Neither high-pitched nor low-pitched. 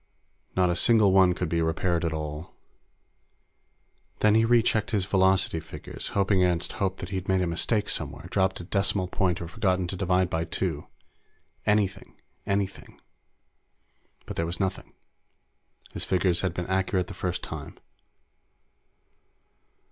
No: very low, 95 Hz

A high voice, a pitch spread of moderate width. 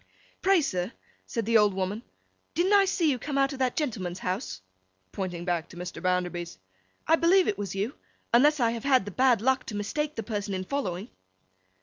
No: high, 225 Hz; wide, 6.9 semitones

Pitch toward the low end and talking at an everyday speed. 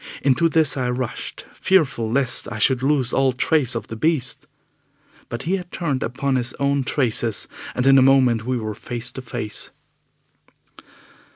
Yes: low, 130 Hz; average, 165 wpm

